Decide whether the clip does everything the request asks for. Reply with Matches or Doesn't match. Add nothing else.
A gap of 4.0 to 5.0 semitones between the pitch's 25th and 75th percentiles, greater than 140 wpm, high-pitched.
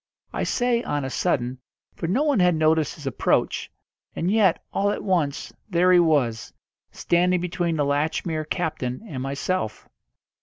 Doesn't match